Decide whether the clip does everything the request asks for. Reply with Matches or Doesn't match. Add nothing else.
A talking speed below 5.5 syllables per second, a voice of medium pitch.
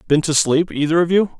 Doesn't match